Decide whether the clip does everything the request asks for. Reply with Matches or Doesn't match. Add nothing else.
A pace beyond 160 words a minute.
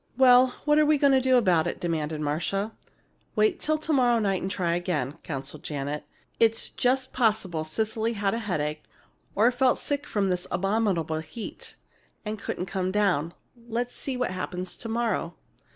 Matches